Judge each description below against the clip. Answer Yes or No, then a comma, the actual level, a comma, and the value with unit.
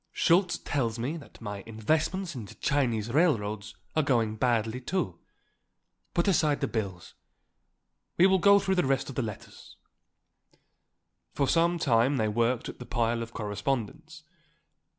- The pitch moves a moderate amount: No, wide, 6.1 semitones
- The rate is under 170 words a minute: Yes, average, 150 wpm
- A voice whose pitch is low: Yes, low, 125 Hz